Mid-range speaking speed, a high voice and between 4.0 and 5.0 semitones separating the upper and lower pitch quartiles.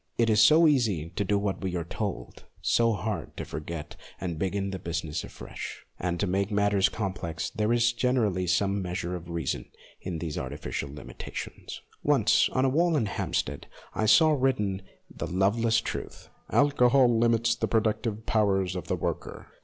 No: average, 175 wpm; low, 100 Hz; average, 4.6 semitones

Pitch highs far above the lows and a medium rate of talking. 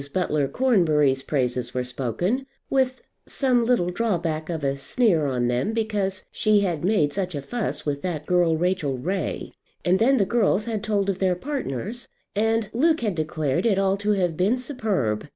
Yes: wide, 6.7 semitones; average, 175 wpm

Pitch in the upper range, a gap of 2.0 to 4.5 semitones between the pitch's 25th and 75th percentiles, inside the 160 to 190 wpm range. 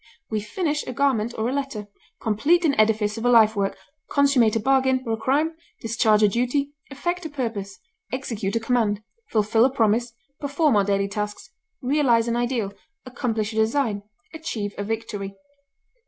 Yes: high, 230 Hz; average, 4.2 semitones; average, 170 wpm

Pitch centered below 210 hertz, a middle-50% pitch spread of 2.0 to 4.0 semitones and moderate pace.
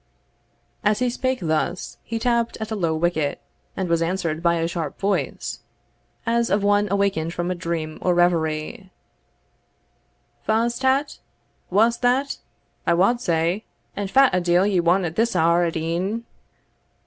No: medium, 185 Hz; average, 5.1 semitones; average, 155 wpm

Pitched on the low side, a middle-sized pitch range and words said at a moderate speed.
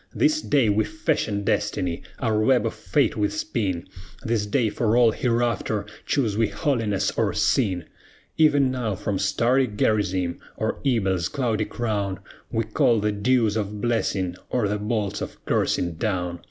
Yes: low, 110 Hz; average, 3.3 semitones; average, 155 wpm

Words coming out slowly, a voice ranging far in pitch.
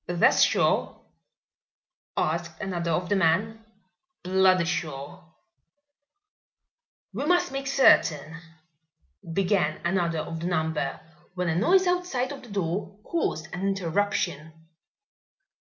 No: slow, 110 wpm; average, 4.2 semitones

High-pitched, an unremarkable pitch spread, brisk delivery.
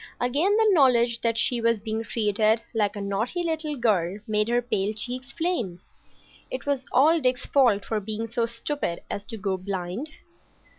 No: high, 230 Hz; average, 4.0 semitones; average, 170 wpm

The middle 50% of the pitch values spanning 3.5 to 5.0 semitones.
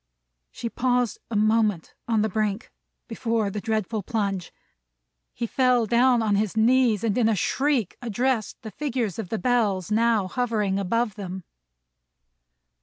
No: average, 2.7 semitones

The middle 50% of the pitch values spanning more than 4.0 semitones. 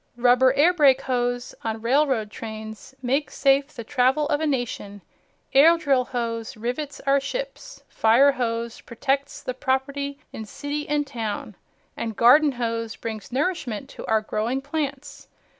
No: average, 3.7 semitones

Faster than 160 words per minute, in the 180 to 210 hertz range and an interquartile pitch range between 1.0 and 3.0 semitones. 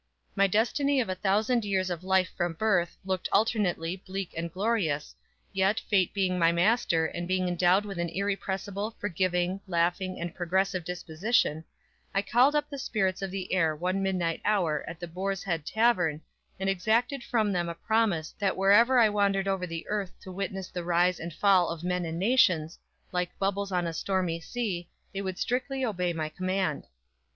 Yes: average, 180 wpm; medium, 185 Hz; average, 2.7 semitones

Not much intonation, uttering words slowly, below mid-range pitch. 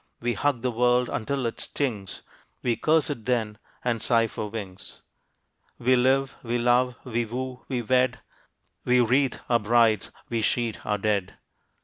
No: narrow, 2.2 semitones; average, 155 wpm; low, 120 Hz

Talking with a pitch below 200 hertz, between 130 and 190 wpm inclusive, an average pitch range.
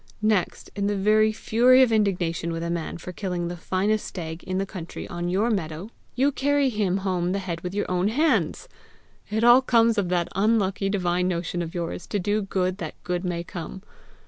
No: high, 190 Hz; average, 200 wpm; average, 3.6 semitones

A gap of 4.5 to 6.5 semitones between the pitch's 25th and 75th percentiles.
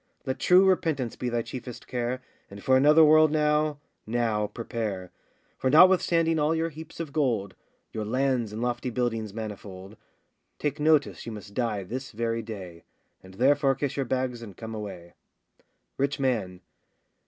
Yes: average, 5.1 semitones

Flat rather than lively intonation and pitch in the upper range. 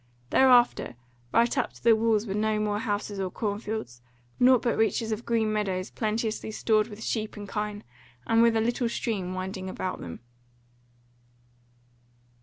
Yes: narrow, 1.9 semitones; high, 215 Hz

